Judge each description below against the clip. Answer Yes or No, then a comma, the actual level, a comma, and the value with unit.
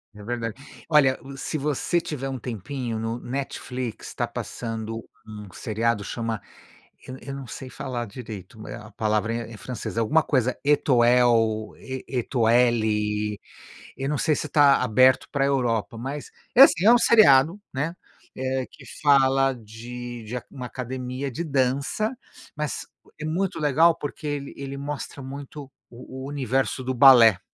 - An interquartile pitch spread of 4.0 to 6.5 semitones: No, average, 3.4 semitones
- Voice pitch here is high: No, low, 130 Hz